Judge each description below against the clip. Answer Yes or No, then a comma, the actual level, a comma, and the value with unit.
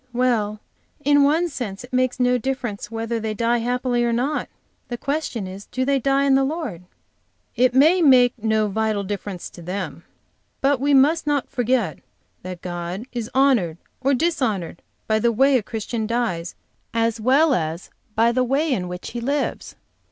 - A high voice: Yes, high, 240 Hz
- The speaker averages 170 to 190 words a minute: Yes, average, 175 wpm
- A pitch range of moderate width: Yes, average, 4.4 semitones